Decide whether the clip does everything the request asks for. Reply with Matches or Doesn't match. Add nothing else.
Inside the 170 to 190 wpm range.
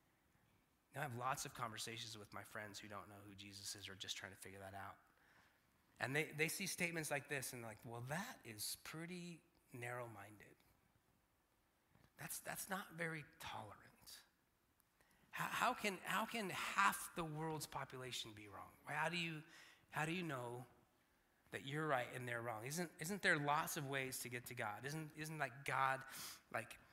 Matches